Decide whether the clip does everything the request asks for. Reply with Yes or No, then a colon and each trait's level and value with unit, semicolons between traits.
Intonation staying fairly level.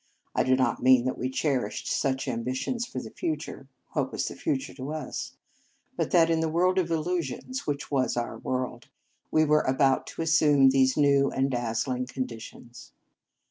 No: average, 3.9 semitones